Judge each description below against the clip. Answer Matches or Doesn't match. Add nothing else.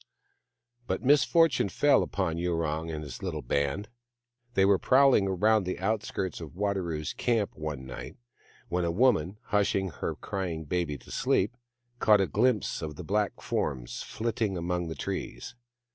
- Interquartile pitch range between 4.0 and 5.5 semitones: Matches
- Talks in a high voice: Doesn't match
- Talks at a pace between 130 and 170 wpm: Matches